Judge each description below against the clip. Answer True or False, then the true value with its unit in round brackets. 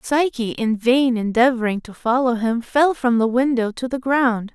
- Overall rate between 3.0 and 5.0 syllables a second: True (4.5 syllables/s)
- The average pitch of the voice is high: True (245 Hz)